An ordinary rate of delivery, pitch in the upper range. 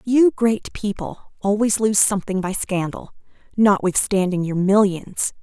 No: slow, 120 wpm; high, 200 Hz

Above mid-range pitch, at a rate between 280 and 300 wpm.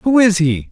No: high, 200 Hz; fast, 255 wpm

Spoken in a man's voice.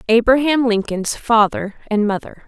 No: female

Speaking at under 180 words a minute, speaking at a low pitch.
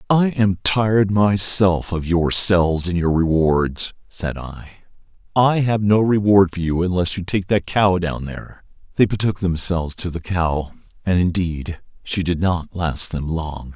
Yes: average, 165 wpm; very low, 90 Hz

